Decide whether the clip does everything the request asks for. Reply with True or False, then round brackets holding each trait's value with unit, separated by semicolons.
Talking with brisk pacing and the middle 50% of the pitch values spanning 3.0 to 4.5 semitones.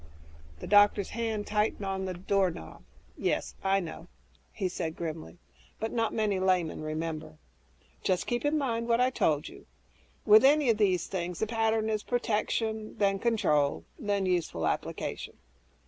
False (150 wpm; 4.1 semitones)